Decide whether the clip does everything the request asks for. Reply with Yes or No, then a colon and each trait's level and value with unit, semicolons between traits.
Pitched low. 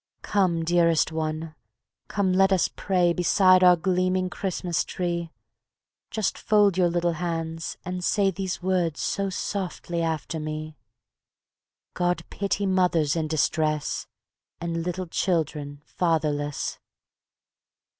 No: medium, 175 Hz